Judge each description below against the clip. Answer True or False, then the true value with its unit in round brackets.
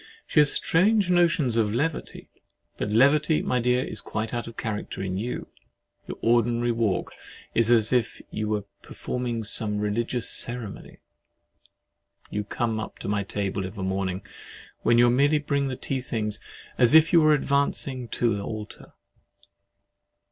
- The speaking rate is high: False (160 wpm)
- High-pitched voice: False (120 Hz)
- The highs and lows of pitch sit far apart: False (4.4 semitones)